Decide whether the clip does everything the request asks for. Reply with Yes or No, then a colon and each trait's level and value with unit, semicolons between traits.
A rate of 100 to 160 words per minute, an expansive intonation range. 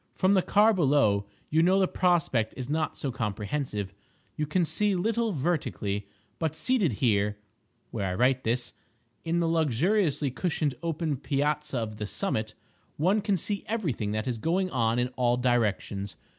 Yes: average, 155 wpm; wide, 7.6 semitones